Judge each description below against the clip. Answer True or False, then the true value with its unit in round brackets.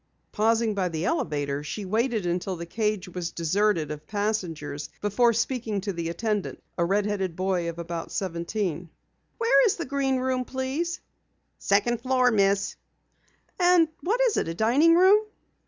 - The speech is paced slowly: False (155 wpm)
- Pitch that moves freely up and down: True (6.6 semitones)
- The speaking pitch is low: False (205 Hz)